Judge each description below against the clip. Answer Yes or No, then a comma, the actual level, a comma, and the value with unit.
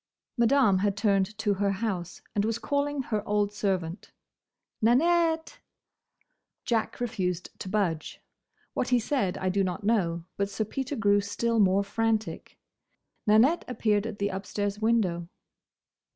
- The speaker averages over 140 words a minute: No, slow, 135 wpm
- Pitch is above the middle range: Yes, high, 210 Hz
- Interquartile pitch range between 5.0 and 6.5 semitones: No, average, 3.0 semitones